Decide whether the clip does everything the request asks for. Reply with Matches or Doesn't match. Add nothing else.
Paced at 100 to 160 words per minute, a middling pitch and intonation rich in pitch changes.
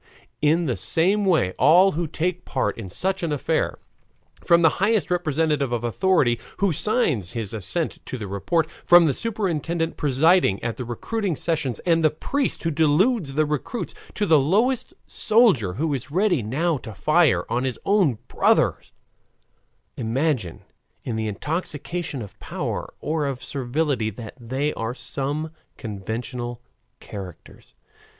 Matches